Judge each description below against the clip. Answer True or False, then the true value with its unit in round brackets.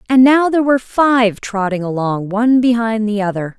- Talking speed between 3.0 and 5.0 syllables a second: False (5.3 syllables/s)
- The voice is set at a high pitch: True (225 Hz)